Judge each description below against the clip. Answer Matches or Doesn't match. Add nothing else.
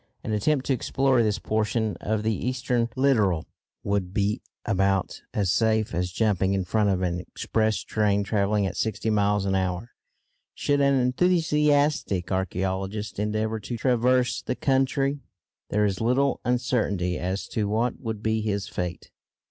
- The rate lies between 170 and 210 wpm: Doesn't match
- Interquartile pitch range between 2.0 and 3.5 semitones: Doesn't match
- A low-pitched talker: Matches